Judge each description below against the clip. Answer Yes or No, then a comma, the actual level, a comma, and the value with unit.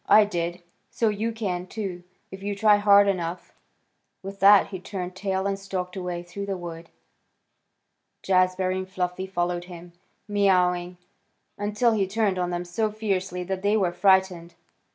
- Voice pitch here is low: No, high, 190 Hz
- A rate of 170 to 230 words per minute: No, average, 155 wpm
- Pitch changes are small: Yes, narrow, 2.1 semitones